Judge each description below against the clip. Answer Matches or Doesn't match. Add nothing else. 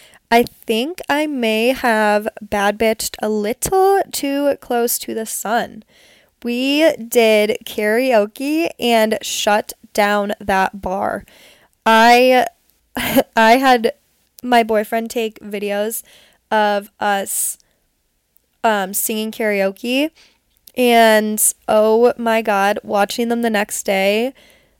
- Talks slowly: Matches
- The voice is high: Matches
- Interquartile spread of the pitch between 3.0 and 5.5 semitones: Doesn't match